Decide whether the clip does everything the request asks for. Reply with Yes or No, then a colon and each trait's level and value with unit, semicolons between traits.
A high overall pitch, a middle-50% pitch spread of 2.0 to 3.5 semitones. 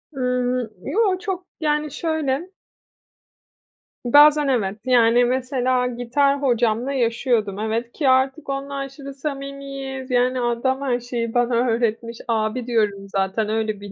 Yes: very high, 250 Hz; average, 3.1 semitones